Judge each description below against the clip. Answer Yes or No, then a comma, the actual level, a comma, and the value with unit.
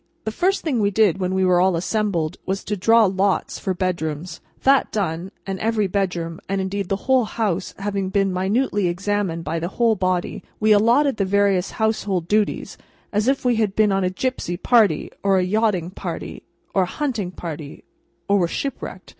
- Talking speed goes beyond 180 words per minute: Yes, average, 190 wpm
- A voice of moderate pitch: No, high, 195 Hz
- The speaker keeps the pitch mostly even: No, average, 3.0 semitones